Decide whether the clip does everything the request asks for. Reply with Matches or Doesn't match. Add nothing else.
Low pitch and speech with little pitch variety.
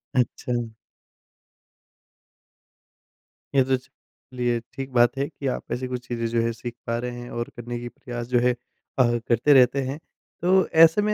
Matches